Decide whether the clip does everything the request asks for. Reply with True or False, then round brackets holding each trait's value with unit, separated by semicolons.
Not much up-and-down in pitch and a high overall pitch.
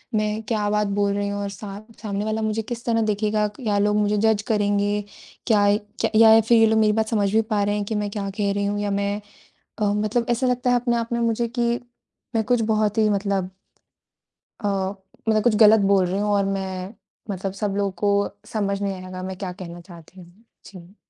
True (1.7 semitones; 210 Hz)